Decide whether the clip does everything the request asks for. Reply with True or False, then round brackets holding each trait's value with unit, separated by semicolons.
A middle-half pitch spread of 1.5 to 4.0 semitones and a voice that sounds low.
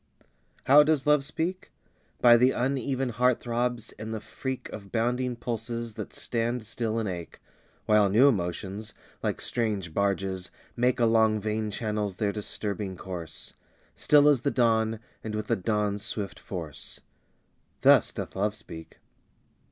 True (3.3 semitones; 110 Hz)